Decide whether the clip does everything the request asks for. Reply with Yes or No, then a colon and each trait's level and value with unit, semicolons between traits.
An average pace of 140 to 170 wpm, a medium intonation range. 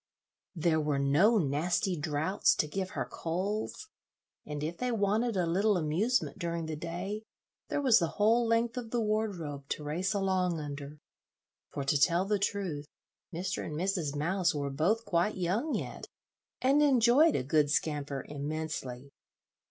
No: average, 155 wpm; wide, 5.9 semitones